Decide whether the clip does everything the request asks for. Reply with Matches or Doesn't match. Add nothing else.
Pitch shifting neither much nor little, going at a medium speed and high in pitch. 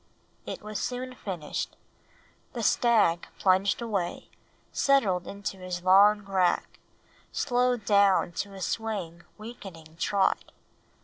Doesn't match